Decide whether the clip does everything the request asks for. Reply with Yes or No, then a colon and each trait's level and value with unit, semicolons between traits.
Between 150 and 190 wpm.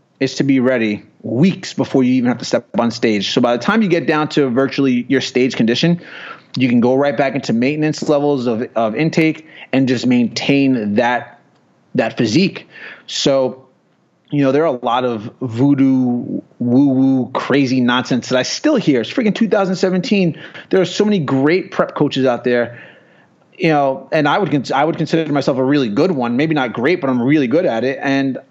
No: average, 200 wpm